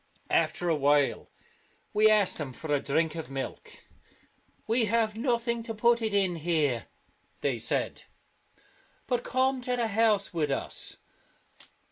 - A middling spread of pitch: No, wide, 7.6 semitones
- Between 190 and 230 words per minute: No, average, 150 wpm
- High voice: Yes, high, 200 Hz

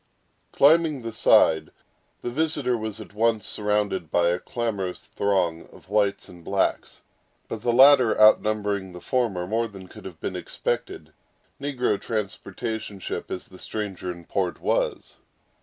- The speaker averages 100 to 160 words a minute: Yes, average, 145 wpm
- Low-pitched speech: Yes, low, 105 Hz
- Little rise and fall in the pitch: No, average, 3.8 semitones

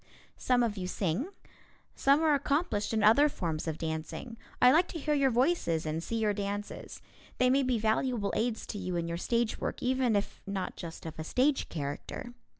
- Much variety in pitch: Yes, wide, 6.3 semitones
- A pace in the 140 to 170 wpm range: No, average, 195 wpm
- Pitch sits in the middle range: No, high, 220 Hz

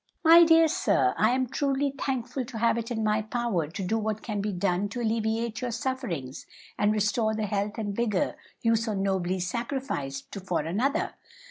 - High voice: Yes, high, 220 Hz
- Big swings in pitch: No, average, 3.4 semitones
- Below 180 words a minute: No, average, 185 wpm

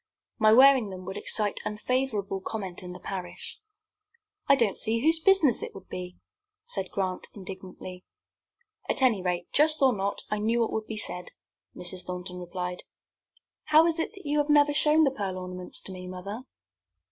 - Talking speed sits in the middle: Yes, average, 170 wpm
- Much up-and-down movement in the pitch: Yes, wide, 6.6 semitones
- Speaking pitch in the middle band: No, high, 205 Hz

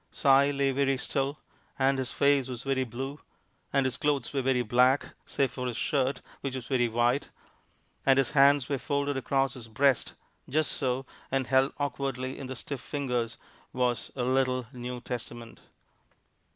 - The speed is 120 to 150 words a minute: No, average, 165 wpm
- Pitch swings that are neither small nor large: No, narrow, 1.8 semitones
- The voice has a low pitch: Yes, low, 130 Hz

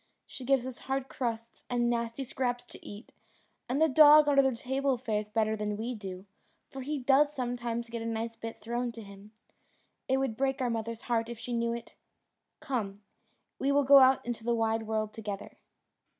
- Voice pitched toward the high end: Yes, high, 235 Hz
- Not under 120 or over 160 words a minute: No, average, 195 wpm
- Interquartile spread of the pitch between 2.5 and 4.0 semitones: Yes, average, 2.9 semitones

